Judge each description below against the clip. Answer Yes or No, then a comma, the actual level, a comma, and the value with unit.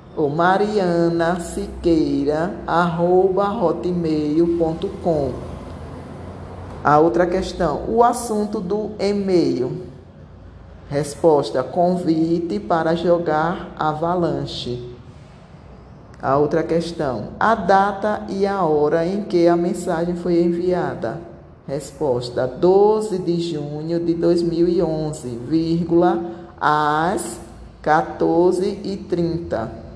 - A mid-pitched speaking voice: Yes, medium, 170 Hz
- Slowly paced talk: Yes, slow, 80 wpm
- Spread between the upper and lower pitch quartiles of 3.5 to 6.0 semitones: No, average, 2.8 semitones